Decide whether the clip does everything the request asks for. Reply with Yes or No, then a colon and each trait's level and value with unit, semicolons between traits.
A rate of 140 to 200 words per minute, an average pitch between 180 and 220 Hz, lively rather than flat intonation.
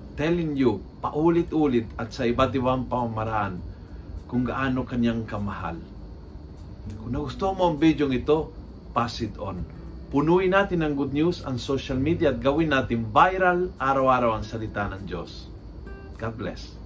No: average, 145 wpm; low, 120 Hz; wide, 6.6 semitones